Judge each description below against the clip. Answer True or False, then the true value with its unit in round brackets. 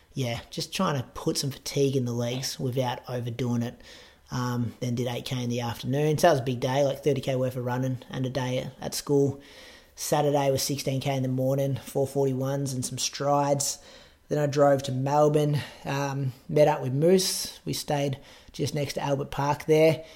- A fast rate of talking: False (190 wpm)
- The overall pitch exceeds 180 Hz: False (140 Hz)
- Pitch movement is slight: True (2.0 semitones)